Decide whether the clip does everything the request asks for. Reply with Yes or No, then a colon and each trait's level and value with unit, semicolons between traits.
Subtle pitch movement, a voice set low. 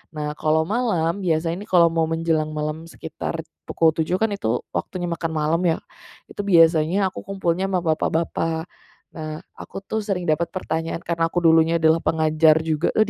No: narrow, 1.7 semitones; medium, 165 Hz